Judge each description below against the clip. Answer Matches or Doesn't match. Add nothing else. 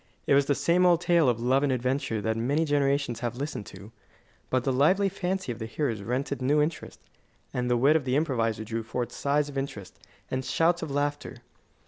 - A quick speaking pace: Matches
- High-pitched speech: Doesn't match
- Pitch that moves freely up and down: Doesn't match